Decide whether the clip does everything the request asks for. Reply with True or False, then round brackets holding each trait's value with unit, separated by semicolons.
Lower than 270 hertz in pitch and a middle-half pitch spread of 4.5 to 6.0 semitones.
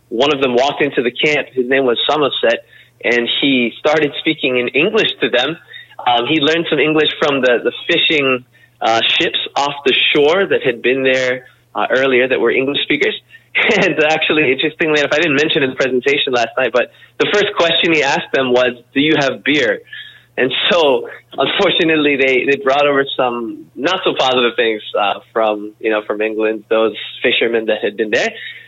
True (140 Hz; 5.1 semitones)